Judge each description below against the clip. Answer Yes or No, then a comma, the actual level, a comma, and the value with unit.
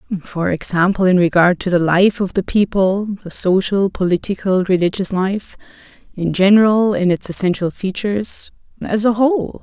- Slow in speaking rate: Yes, slow, 130 wpm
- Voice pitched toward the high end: Yes, high, 195 Hz